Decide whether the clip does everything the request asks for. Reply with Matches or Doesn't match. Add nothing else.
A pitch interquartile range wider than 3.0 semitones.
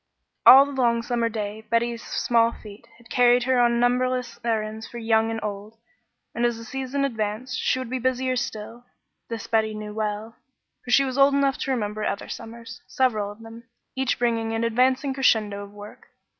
Doesn't match